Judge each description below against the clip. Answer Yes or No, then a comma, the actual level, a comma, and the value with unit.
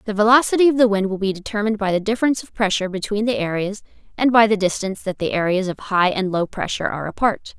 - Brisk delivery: Yes, fast, 235 wpm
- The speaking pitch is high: Yes, high, 205 Hz